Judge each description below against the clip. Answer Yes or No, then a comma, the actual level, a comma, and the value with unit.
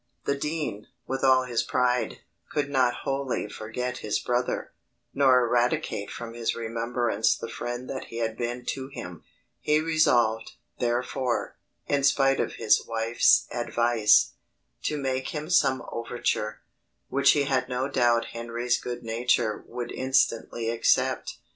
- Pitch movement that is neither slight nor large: No, narrow, 2.3 semitones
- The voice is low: Yes, low, 125 Hz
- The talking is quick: No, average, 140 wpm